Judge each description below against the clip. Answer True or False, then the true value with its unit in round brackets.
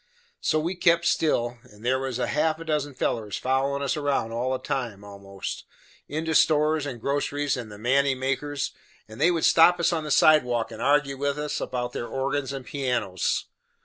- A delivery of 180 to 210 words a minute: True (190 wpm)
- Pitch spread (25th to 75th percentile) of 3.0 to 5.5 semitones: True (3.6 semitones)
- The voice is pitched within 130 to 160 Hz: True (140 Hz)